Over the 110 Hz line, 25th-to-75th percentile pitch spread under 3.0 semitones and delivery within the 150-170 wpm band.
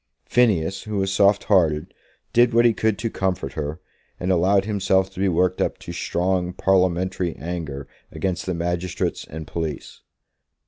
No: very low, 95 Hz; narrow, 2.5 semitones; average, 155 wpm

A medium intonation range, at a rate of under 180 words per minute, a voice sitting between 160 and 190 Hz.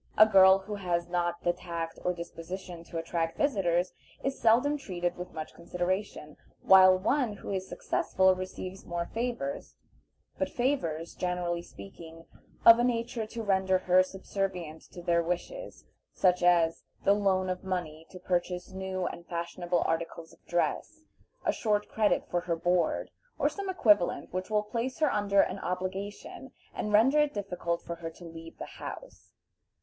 Yes: average, 3.3 semitones; average, 160 wpm; medium, 185 Hz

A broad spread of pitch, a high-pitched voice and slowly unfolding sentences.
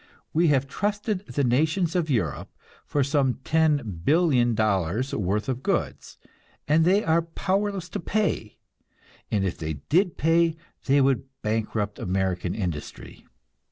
No: wide, 7.7 semitones; medium, 140 Hz; slow, 125 wpm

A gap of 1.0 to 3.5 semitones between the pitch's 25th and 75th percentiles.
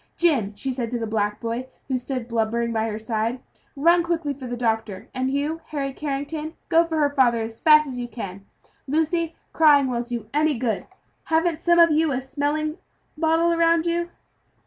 No: average, 5.2 semitones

